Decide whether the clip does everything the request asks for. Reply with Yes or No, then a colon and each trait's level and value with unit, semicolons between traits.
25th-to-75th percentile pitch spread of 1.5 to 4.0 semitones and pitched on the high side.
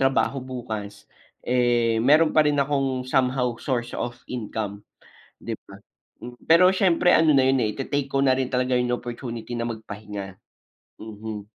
No: average, 3.3 semitones; low, 125 Hz